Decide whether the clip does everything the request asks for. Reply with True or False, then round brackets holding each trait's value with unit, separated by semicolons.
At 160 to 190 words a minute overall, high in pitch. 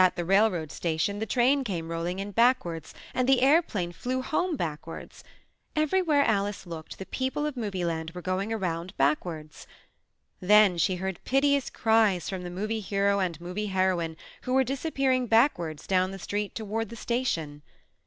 True (170 wpm; 200 Hz)